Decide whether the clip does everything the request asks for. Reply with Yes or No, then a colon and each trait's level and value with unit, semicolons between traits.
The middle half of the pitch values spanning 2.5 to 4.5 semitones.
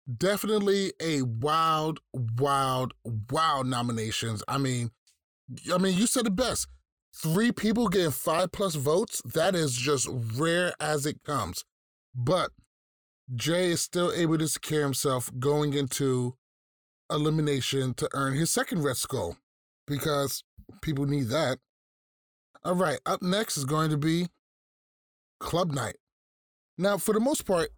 No: average, 5.2 semitones